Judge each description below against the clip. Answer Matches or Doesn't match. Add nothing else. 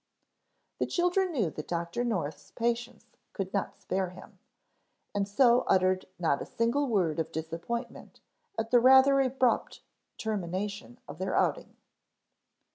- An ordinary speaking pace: Doesn't match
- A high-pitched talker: Matches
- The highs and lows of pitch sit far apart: Matches